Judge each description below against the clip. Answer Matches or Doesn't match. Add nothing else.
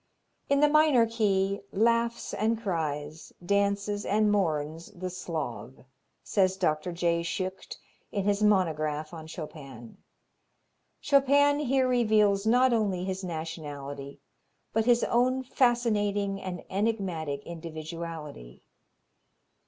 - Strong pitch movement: Matches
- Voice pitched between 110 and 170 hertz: Doesn't match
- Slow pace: Matches